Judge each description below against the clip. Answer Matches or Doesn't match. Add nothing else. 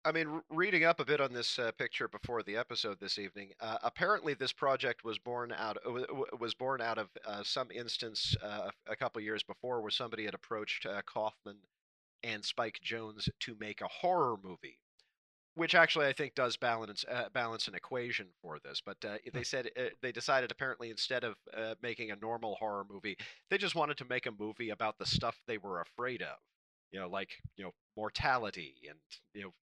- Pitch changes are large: Doesn't match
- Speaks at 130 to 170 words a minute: Doesn't match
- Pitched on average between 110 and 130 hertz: Matches